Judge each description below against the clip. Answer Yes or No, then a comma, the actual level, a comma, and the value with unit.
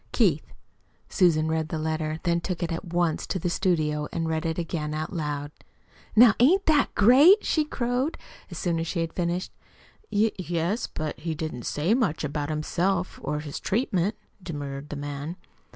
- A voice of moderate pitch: Yes, medium, 165 Hz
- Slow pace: No, average, 170 wpm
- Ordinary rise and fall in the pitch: Yes, average, 3.8 semitones